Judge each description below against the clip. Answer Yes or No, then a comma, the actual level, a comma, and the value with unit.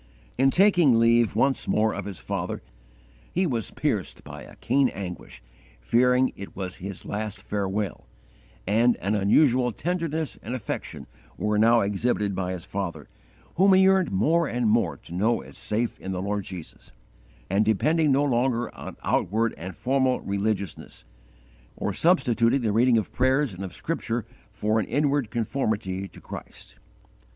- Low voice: Yes, low, 115 Hz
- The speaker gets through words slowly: No, average, 155 wpm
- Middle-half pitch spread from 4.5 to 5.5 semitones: Yes, average, 4.8 semitones